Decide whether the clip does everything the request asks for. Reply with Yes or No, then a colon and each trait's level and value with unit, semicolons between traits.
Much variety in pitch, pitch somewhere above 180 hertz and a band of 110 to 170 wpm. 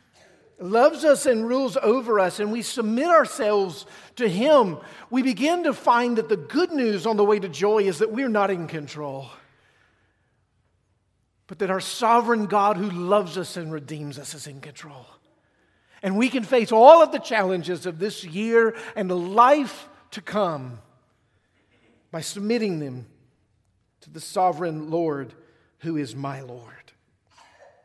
Yes: wide, 8.3 semitones; high, 190 Hz; average, 155 wpm